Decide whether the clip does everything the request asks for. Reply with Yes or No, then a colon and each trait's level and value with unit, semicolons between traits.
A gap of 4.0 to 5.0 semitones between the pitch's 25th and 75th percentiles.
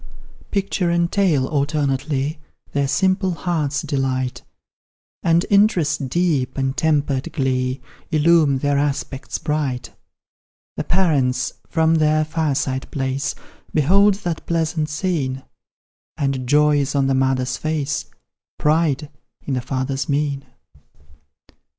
No: average, 3.2 semitones